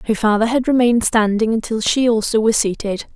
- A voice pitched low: No, high, 225 Hz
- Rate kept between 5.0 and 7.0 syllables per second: Yes, 5.8 syllables/s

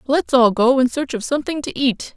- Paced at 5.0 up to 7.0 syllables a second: Yes, 5.5 syllables/s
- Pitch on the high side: Yes, very high, 260 Hz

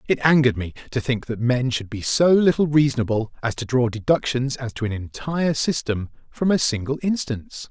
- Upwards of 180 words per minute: Yes, average, 195 wpm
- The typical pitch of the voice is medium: No, low, 130 Hz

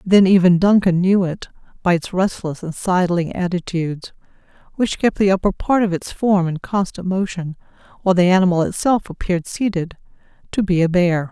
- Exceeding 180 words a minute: No, average, 170 wpm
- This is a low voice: No, medium, 185 Hz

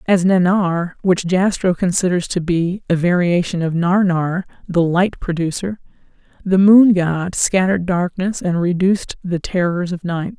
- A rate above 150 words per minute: No, average, 145 wpm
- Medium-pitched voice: Yes, medium, 180 Hz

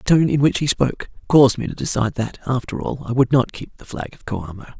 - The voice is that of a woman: No, male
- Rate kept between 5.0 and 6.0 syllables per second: No, 6.3 syllables/s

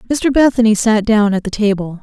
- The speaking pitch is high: Yes, high, 220 Hz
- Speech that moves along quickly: Yes, fast, 210 wpm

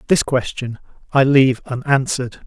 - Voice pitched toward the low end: Yes, low, 130 Hz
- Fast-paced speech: No, slow, 120 wpm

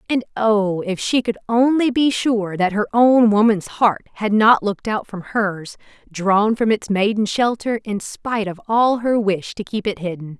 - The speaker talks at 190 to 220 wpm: Yes, average, 195 wpm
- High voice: Yes, high, 215 Hz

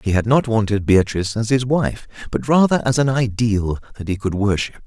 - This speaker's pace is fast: Yes, fast, 210 wpm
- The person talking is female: No, male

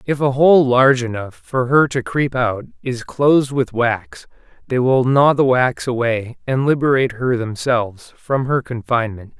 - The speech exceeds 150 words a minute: Yes, average, 170 wpm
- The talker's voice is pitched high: No, low, 125 Hz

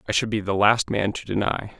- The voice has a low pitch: Yes, low, 105 Hz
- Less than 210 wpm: No, fast, 265 wpm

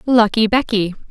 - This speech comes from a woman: Yes, female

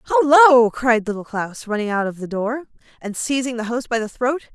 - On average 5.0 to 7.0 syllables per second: Yes, 5.1 syllables/s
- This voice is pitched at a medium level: No, high, 240 Hz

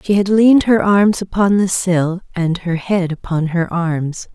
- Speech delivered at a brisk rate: No, average, 195 wpm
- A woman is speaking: Yes, female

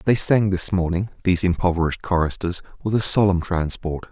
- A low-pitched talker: Yes, very low, 90 Hz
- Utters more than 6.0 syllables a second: No, 5.5 syllables/s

